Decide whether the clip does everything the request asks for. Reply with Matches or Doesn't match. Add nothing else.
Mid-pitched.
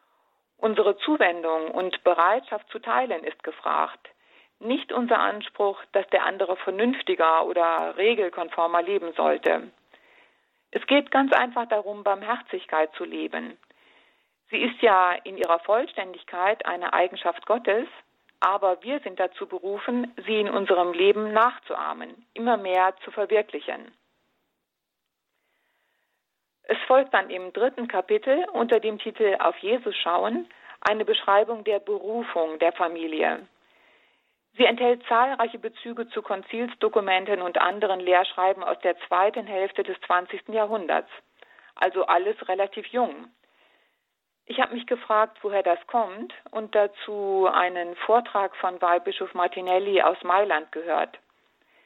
Doesn't match